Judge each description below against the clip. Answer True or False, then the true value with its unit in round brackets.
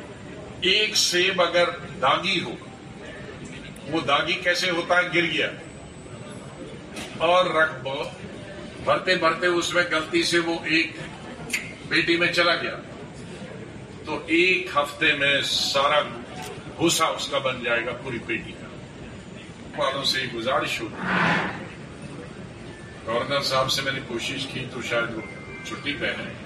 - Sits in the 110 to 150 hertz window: False (165 Hz)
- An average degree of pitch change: True (4.4 semitones)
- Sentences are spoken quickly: False (130 wpm)